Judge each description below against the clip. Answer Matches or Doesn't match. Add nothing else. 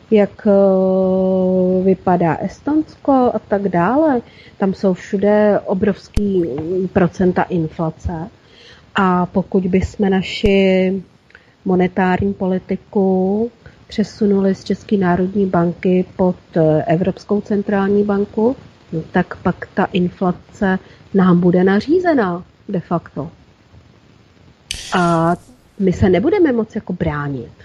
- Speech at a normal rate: Doesn't match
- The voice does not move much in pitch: Matches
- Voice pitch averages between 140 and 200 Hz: Matches